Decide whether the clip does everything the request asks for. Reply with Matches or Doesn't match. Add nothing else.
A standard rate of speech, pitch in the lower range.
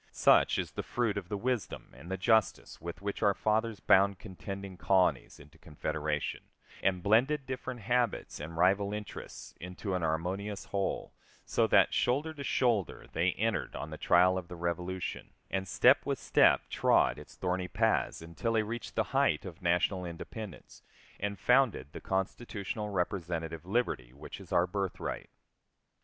Matches